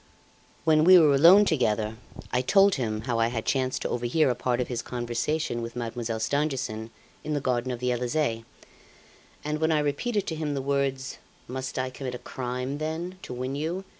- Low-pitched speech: Yes, low, 130 Hz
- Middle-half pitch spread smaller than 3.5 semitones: No, average, 4.1 semitones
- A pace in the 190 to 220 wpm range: Yes, average, 195 wpm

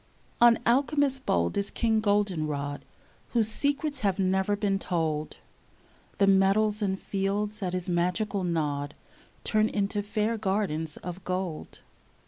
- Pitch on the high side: Yes, high, 195 Hz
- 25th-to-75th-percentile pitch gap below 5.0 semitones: Yes, average, 3.3 semitones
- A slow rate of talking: Yes, slow, 125 wpm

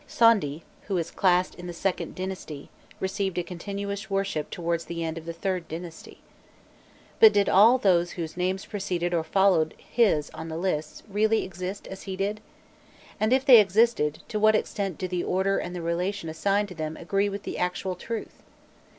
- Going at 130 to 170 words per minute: No, average, 185 wpm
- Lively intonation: No, average, 3.0 semitones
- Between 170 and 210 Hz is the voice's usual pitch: Yes, medium, 185 Hz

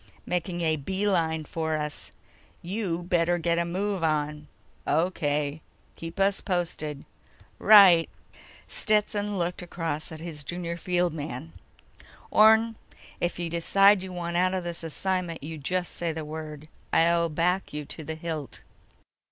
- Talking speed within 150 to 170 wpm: No, average, 140 wpm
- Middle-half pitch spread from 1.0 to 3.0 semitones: Yes, narrow, 2.6 semitones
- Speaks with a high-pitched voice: No, medium, 170 Hz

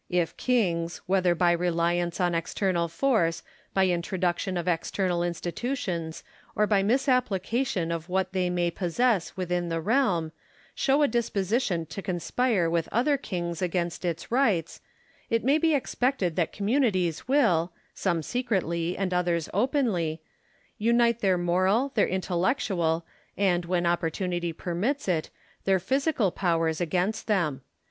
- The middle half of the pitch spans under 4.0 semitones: No, average, 4.7 semitones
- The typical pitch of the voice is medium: Yes, medium, 180 Hz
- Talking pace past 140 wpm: No, slow, 135 wpm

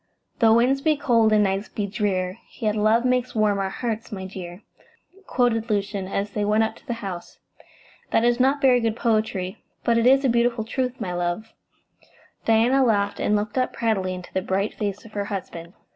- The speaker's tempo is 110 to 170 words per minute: No, average, 195 wpm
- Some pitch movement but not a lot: Yes, average, 3.2 semitones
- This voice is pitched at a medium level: No, high, 215 Hz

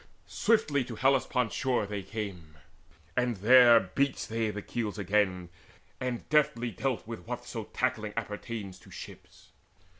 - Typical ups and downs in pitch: Yes, average, 3.4 semitones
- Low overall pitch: Yes, low, 115 Hz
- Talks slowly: Yes, slow, 130 wpm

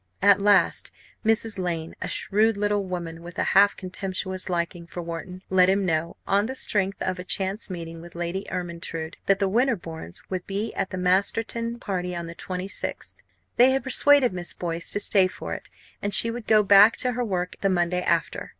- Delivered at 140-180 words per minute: No, average, 195 wpm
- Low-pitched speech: No, high, 190 Hz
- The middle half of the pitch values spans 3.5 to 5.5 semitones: No, average, 2.9 semitones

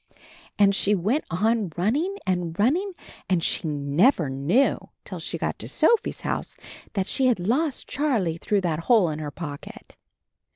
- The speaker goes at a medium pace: Yes, average, 165 wpm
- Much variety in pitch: Yes, wide, 7.2 semitones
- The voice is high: Yes, high, 195 Hz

